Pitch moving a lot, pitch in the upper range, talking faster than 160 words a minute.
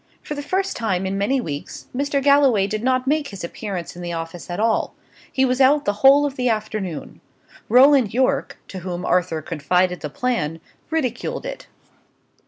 Yes: wide, 7.1 semitones; high, 220 Hz; average, 180 wpm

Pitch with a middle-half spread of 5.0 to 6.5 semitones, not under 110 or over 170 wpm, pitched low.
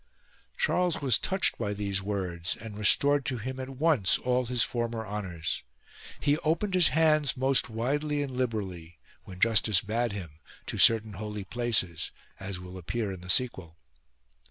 Yes: wide, 5.4 semitones; average, 155 wpm; low, 115 Hz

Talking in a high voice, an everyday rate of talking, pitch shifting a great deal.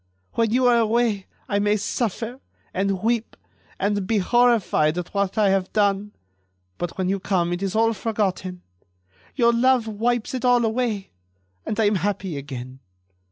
No: high, 205 Hz; average, 160 wpm; average, 3.5 semitones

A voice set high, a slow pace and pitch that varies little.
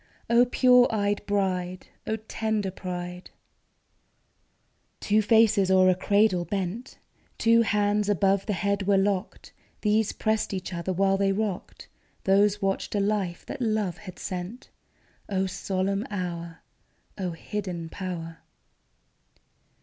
Yes: high, 195 Hz; slow, 125 wpm; narrow, 2.3 semitones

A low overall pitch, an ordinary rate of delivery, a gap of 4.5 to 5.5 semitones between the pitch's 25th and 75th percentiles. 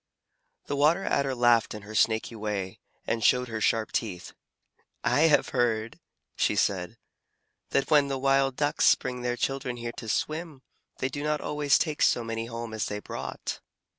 No: low, 125 Hz; average, 170 wpm; average, 4.1 semitones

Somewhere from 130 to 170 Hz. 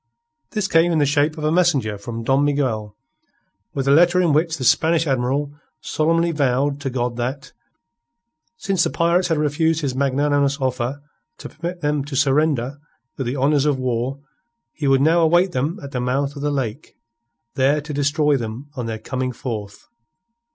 Yes: medium, 140 Hz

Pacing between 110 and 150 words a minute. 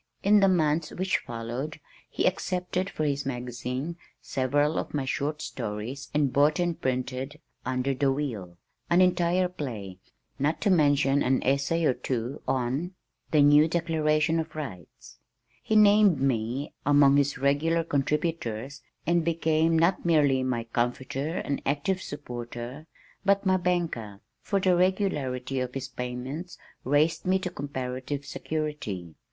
Yes: average, 140 wpm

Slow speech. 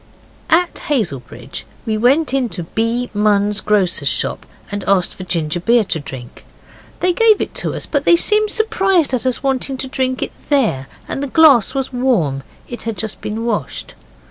No: average, 170 wpm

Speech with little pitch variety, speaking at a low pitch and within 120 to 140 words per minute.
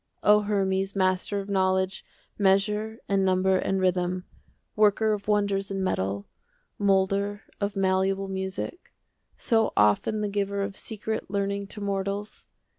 No: narrow, 1.4 semitones; high, 195 Hz; slow, 135 wpm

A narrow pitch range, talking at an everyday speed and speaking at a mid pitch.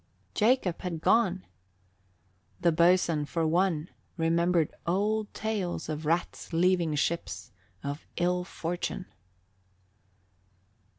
No: narrow, 2.2 semitones; slow, 95 wpm; medium, 175 Hz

